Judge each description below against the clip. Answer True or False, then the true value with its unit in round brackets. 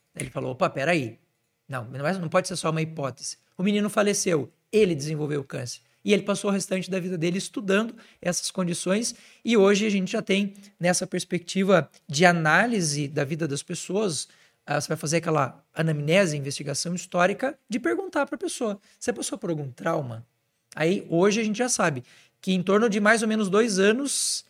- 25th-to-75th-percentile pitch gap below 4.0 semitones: False (5.0 semitones)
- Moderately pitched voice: True (180 Hz)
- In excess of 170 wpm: True (185 wpm)